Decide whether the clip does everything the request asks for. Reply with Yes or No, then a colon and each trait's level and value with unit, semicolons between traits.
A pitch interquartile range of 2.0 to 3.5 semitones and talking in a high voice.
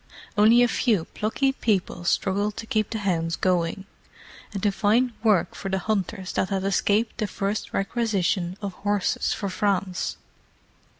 Yes: narrow, 2.4 semitones; high, 200 Hz